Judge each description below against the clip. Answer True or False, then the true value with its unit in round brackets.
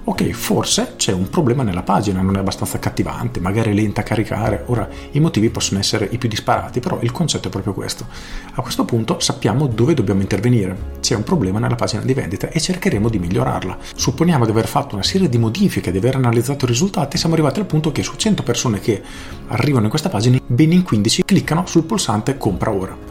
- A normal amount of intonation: False (7.0 semitones)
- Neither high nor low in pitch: False (120 Hz)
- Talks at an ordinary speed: False (215 wpm)